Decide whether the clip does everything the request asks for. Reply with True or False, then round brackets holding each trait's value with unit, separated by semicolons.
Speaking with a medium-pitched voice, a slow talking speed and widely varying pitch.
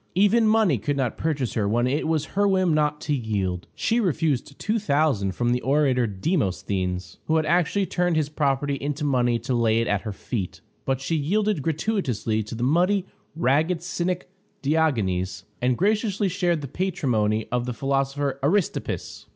False (145 Hz; 165 wpm; 6.5 semitones)